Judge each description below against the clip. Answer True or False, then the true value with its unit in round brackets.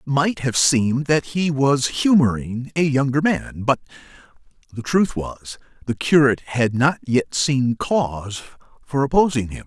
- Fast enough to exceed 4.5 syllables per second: False (4.3 syllables/s)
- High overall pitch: False (135 Hz)